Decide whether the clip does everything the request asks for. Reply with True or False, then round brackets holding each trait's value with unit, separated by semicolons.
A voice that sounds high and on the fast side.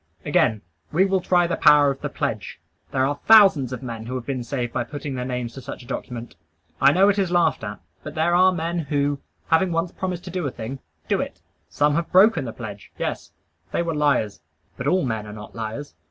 False (145 Hz; 220 wpm)